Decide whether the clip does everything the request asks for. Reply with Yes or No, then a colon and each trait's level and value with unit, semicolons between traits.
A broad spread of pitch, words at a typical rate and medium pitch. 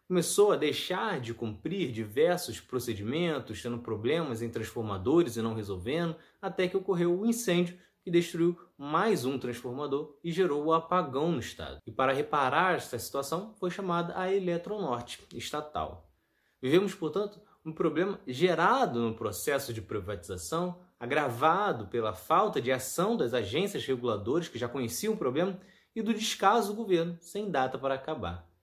Yes: wide, 7.2 semitones; average, 155 wpm; medium, 160 Hz